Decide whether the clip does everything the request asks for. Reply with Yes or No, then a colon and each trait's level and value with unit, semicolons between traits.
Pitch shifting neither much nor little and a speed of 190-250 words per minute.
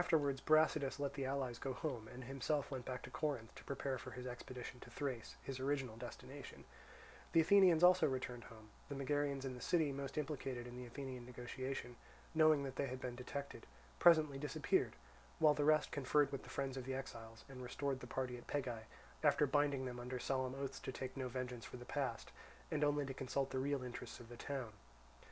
No: narrow, 2.3 semitones; fast, 205 wpm